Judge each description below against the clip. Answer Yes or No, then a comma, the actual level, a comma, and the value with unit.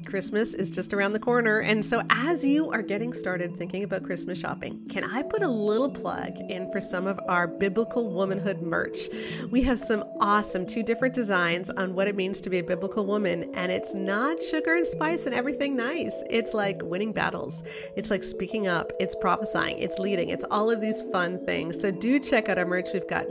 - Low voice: No, high, 200 Hz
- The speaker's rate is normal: No, fast, 210 wpm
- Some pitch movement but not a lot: Yes, average, 4.1 semitones